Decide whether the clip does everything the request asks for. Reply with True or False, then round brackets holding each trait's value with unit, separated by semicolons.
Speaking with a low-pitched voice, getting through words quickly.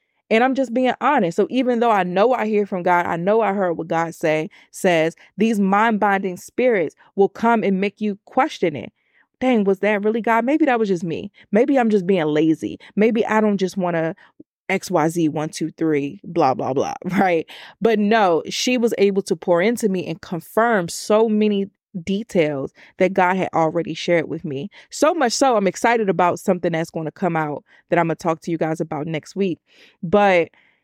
False (195 Hz; 210 wpm)